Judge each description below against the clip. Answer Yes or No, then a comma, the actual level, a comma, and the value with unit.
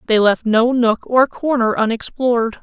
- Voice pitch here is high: Yes, high, 235 Hz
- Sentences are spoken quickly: No, average, 160 wpm